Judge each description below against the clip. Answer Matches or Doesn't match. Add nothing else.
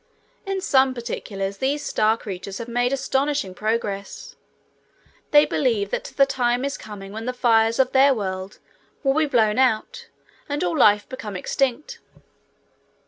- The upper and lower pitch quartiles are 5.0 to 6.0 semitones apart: Doesn't match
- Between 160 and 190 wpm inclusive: Doesn't match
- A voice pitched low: Doesn't match